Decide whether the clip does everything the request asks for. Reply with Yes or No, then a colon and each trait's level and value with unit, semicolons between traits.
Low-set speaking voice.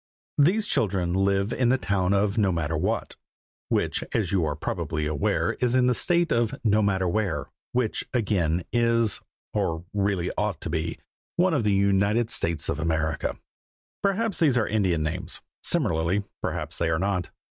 Yes: low, 100 Hz